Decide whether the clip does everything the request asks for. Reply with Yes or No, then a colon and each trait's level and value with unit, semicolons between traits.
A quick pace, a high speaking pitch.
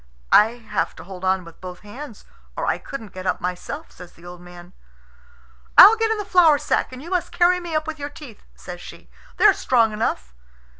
Yes: fast, 210 wpm; high, 225 Hz